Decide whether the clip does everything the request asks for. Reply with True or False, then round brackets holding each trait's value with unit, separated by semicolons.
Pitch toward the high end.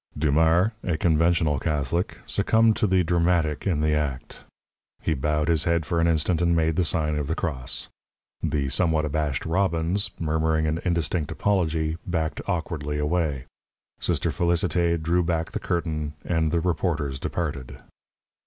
False (80 Hz)